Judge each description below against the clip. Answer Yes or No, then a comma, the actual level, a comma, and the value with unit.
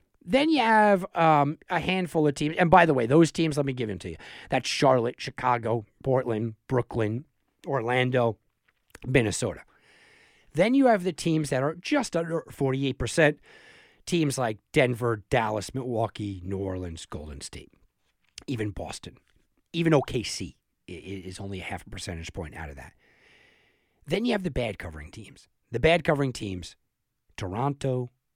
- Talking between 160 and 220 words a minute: No, average, 150 wpm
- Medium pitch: No, low, 130 Hz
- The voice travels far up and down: Yes, wide, 8.2 semitones